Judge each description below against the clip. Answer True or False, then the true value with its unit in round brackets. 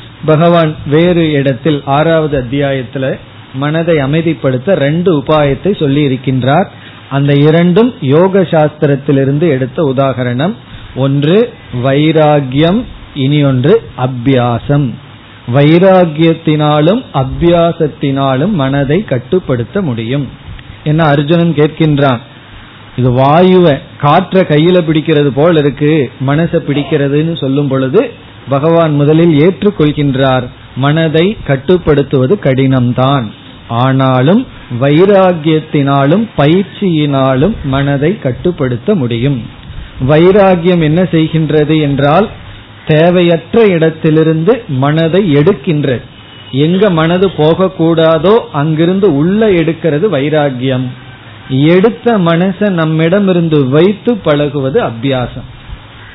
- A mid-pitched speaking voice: True (150 Hz)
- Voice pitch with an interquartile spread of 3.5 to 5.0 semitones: True (4.0 semitones)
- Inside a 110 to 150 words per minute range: False (80 wpm)